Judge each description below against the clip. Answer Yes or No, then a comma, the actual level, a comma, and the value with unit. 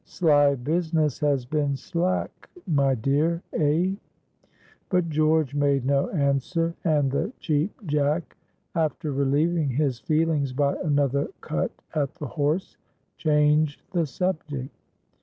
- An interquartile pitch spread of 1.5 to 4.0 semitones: Yes, narrow, 2.6 semitones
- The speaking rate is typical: No, slow, 120 wpm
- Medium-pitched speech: Yes, medium, 150 Hz